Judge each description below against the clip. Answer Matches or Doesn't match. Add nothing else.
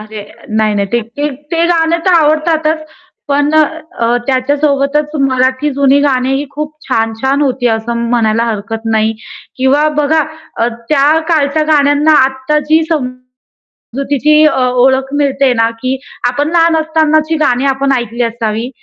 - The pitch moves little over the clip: Doesn't match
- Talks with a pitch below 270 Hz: Doesn't match